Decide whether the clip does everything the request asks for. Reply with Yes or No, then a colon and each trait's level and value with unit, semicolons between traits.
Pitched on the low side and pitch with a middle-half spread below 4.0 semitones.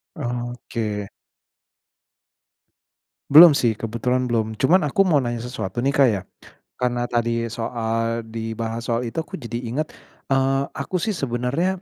Yes: low, 120 Hz; average, 3.1 semitones